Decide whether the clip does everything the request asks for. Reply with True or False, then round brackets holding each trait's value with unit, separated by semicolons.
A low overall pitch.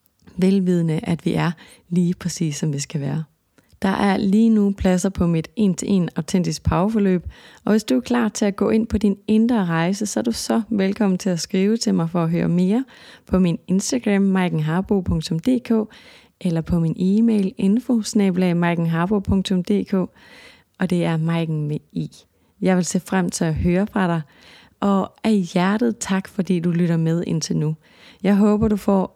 False (190 Hz)